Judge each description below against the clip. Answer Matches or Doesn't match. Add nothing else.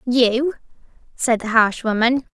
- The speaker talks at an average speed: Doesn't match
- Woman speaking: Matches